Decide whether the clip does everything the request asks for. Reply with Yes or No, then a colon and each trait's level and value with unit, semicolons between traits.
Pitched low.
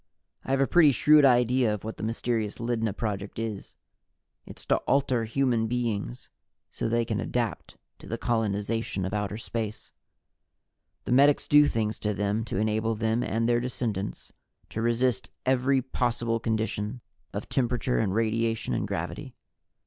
Yes: low, 115 Hz